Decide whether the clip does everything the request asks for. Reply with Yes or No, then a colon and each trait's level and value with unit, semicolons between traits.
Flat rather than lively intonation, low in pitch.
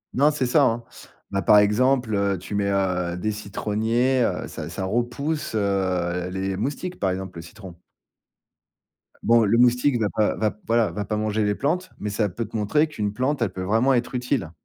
No: average, 4.0 semitones; low, 105 Hz